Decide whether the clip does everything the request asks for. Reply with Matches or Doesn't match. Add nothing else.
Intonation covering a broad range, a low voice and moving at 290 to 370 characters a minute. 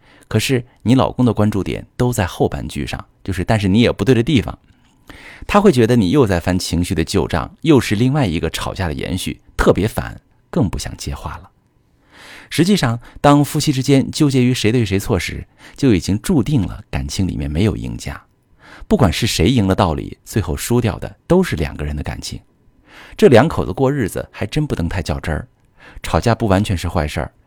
Matches